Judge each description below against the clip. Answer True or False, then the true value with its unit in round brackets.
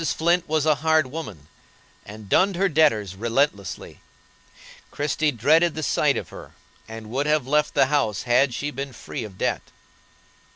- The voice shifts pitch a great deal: True (5.7 semitones)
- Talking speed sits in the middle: True (160 wpm)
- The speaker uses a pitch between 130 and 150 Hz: True (140 Hz)